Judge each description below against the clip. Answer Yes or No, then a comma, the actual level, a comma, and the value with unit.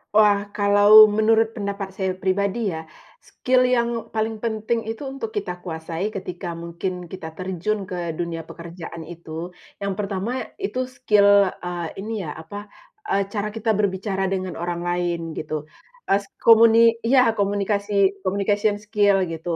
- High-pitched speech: Yes, high, 200 Hz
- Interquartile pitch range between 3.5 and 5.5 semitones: No, average, 3.1 semitones